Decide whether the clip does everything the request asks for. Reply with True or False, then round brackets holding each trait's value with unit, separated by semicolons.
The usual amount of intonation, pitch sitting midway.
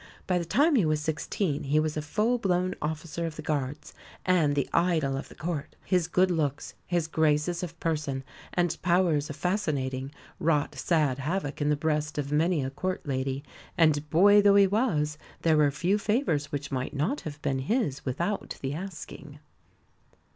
True (3.7 semitones; 155 Hz)